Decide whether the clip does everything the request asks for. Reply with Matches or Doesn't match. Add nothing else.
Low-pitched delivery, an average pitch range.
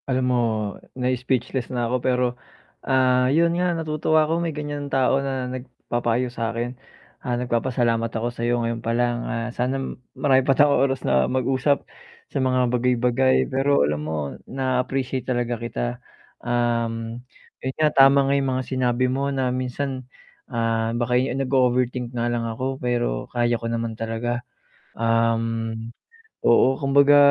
Doesn't match